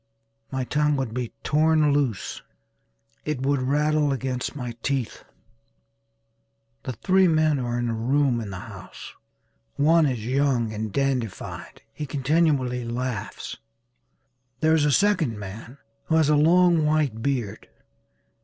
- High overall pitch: No, low, 135 Hz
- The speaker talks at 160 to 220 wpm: No, slow, 135 wpm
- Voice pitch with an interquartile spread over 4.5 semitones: No, average, 4.0 semitones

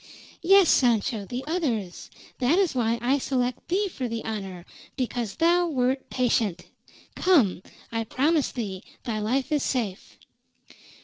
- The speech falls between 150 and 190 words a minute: No, slow, 135 wpm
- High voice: Yes, very high, 250 Hz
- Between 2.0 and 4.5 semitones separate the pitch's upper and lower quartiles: No, average, 5.2 semitones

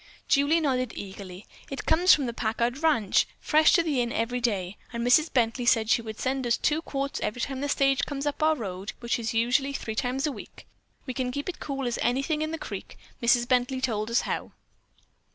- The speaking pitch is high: Yes, very high, 255 Hz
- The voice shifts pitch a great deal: No, average, 3.3 semitones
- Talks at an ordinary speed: No, fast, 215 wpm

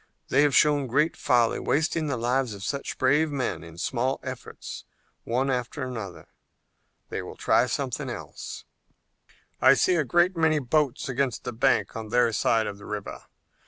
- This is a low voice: Yes, low, 130 Hz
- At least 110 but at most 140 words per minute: No, average, 160 wpm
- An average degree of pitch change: Yes, average, 4.1 semitones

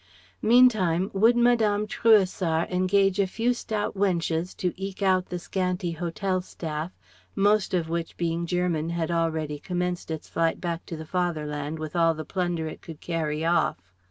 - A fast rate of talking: No, average, 160 wpm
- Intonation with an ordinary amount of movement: Yes, average, 3.0 semitones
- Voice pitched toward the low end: No, medium, 175 Hz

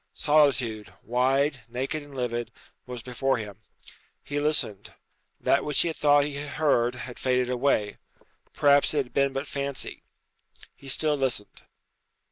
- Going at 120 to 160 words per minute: Yes, average, 140 wpm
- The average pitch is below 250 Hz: Yes, low, 135 Hz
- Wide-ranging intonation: No, average, 2.8 semitones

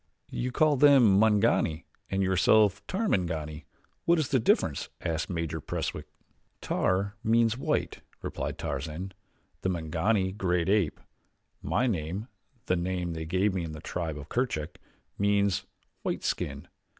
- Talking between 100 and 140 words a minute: Yes, slow, 135 wpm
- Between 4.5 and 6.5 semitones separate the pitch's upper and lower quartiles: Yes, average, 4.8 semitones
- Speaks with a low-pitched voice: Yes, very low, 95 Hz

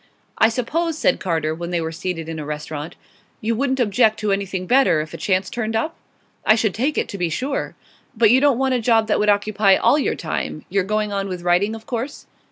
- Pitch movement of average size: Yes, average, 4.9 semitones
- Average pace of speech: No, fast, 230 wpm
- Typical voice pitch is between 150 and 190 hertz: No, high, 210 Hz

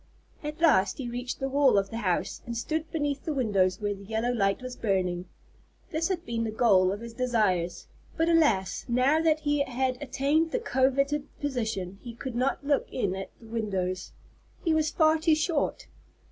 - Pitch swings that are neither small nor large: No, wide, 6.3 semitones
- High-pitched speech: Yes, very high, 250 Hz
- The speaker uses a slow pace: No, average, 190 wpm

